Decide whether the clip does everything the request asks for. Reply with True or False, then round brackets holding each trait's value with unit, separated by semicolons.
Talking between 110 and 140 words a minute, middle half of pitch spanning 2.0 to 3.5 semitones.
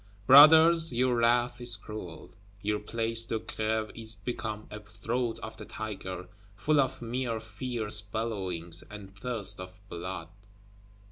True (135 wpm; 2.8 semitones)